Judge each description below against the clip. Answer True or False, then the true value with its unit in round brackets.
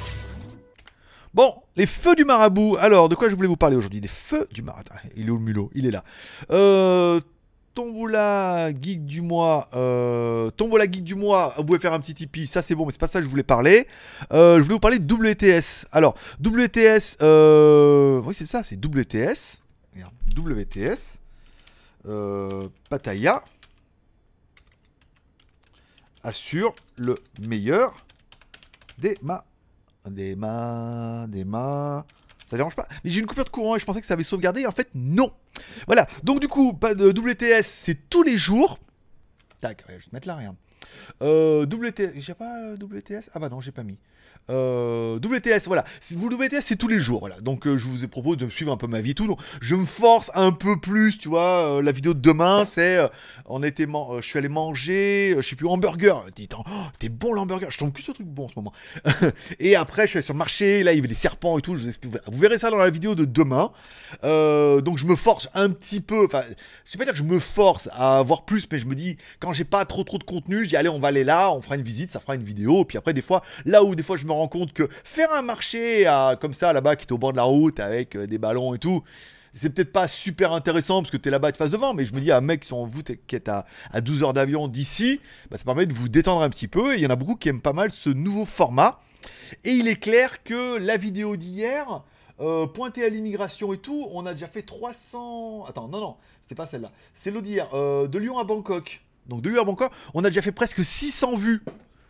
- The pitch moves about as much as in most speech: False (7.6 semitones)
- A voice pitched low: False (165 Hz)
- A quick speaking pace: True (235 wpm)